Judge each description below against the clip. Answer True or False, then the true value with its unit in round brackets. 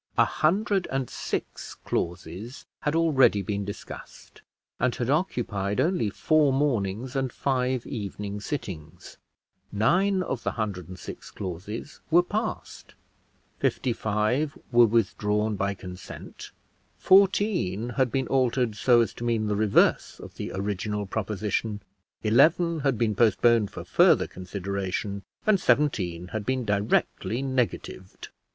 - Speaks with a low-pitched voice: True (115 Hz)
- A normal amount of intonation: True (5.0 semitones)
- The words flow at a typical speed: False (130 wpm)